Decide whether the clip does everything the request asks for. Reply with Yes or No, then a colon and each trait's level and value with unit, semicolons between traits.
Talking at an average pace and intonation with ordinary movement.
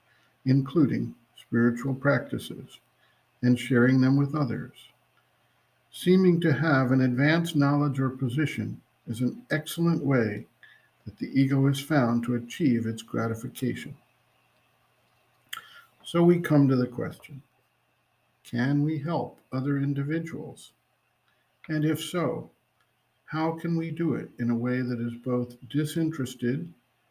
No: slow, 120 wpm; average, 4.0 semitones